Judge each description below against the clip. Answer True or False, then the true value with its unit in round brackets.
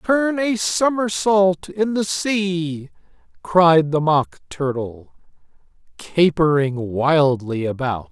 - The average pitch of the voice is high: False (165 Hz)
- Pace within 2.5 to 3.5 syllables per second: True (3.0 syllables/s)